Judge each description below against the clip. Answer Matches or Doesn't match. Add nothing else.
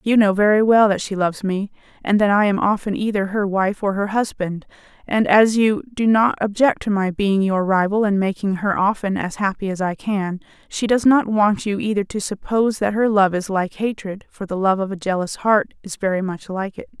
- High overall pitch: Matches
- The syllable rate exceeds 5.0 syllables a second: Matches